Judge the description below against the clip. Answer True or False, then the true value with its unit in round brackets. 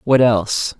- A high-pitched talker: False (115 Hz)